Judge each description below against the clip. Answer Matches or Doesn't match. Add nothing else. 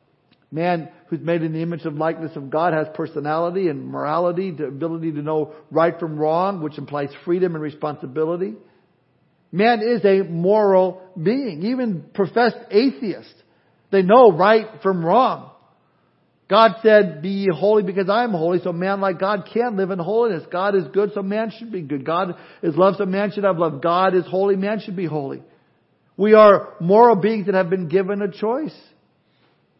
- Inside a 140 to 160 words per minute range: Doesn't match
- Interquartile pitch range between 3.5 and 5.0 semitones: Matches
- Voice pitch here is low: Doesn't match